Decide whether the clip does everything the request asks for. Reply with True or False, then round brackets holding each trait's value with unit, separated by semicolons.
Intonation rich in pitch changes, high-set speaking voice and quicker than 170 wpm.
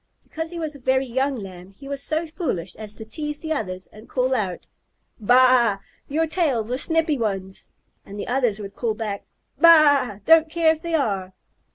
True (6.8 semitones; 255 Hz; 190 wpm)